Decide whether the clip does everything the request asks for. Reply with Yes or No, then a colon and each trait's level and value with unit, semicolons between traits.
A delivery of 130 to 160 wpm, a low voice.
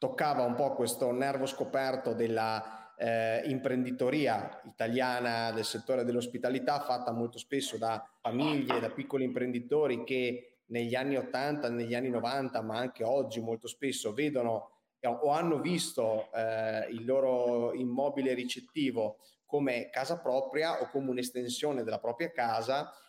Yes: average, 135 wpm; low, 125 Hz